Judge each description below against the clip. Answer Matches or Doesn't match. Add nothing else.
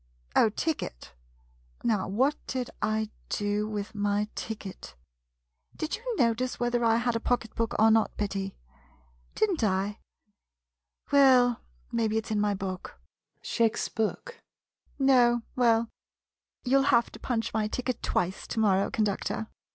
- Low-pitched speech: Doesn't match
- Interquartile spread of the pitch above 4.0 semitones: Doesn't match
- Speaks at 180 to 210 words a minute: Doesn't match